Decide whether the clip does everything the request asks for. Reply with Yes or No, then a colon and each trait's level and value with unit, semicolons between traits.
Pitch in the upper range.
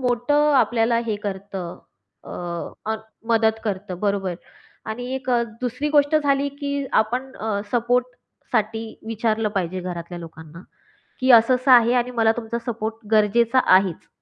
Yes: high, 225 Hz